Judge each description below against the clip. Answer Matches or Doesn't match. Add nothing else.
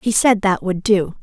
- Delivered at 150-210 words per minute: Doesn't match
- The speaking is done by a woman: Matches